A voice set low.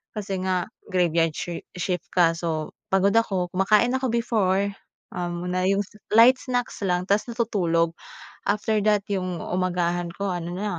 No: medium, 185 Hz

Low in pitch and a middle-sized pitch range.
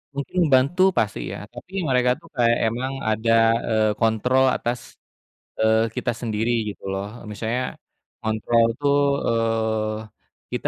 No: low, 115 Hz; narrow, 2.2 semitones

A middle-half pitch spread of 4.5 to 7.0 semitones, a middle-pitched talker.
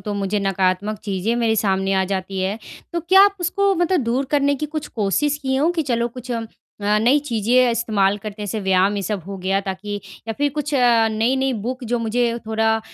No: average, 4.8 semitones; high, 225 Hz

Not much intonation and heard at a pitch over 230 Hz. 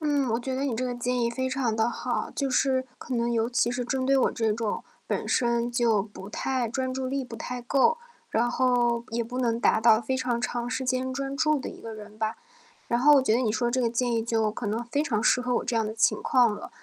Yes: narrow, 2.1 semitones; high, 240 Hz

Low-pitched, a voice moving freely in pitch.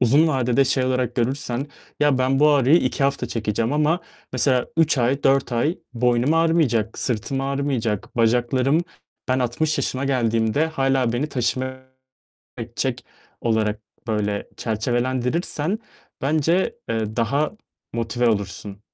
No: low, 130 Hz; average, 3.4 semitones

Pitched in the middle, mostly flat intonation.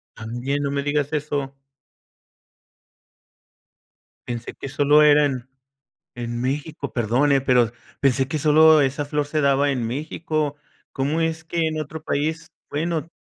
Yes: medium, 145 Hz; narrow, 2.3 semitones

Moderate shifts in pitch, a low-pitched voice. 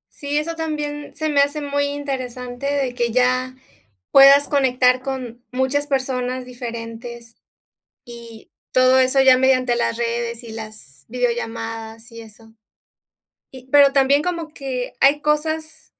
No: average, 3.1 semitones; very high, 255 Hz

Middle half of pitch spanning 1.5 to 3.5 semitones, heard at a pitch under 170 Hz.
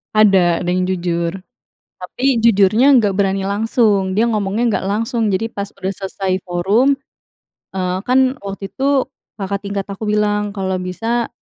No: average, 3.1 semitones; high, 200 Hz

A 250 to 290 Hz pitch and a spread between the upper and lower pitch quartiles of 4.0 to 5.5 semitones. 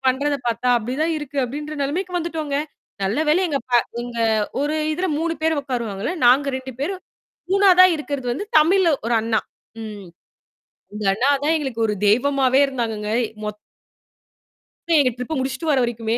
Yes: very high, 270 Hz; average, 4.6 semitones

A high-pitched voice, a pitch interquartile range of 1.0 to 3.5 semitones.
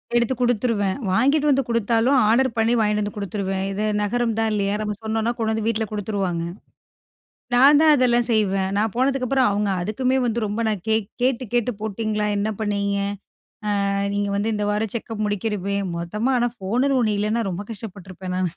Yes: high, 220 Hz; average, 2.8 semitones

